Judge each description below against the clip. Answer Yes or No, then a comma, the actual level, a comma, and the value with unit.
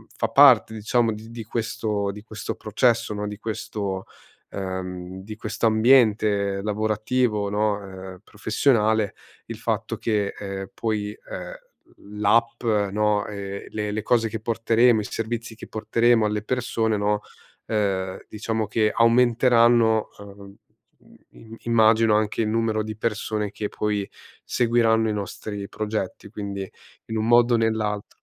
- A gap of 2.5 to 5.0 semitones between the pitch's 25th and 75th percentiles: No, narrow, 1.7 semitones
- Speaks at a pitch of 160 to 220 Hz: No, low, 110 Hz